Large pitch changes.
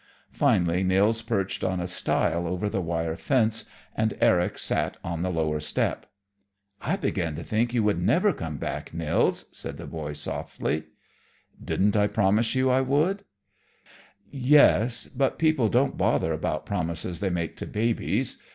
Yes: wide, 6.3 semitones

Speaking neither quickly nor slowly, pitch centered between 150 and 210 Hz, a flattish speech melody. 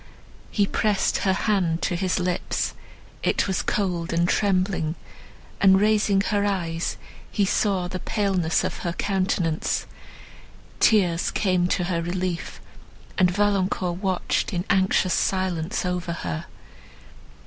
No: slow, 125 wpm; medium, 185 Hz; narrow, 2.2 semitones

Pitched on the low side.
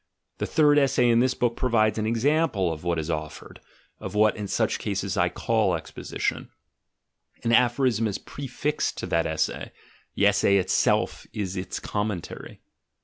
Yes: low, 110 Hz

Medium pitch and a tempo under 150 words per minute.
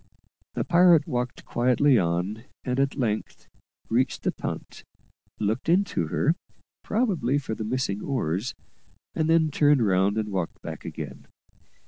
No: low, 125 Hz; slow, 135 wpm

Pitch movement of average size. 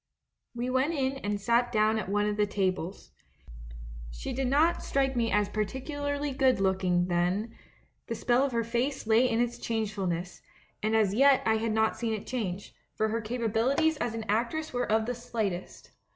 Yes: average, 3.6 semitones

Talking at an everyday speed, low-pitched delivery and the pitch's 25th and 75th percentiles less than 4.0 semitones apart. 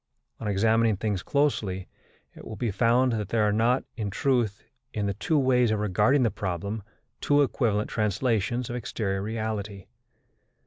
Yes: average, 155 wpm; low, 110 Hz; average, 3.1 semitones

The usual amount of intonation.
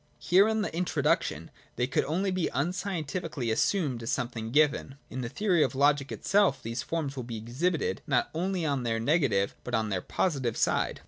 No: wide, 6.7 semitones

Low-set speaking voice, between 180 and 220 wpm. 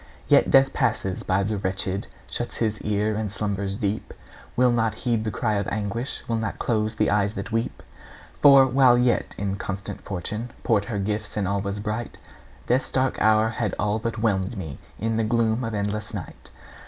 Yes: low, 110 Hz; average, 185 wpm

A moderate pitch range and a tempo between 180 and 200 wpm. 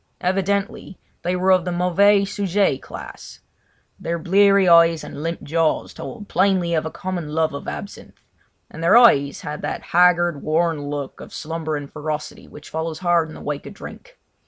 No: average, 3.3 semitones; average, 170 wpm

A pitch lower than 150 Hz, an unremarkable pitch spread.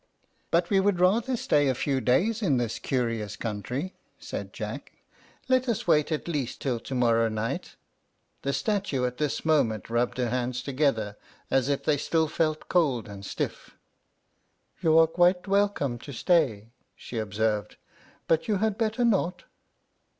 No: medium, 140 Hz; wide, 7.1 semitones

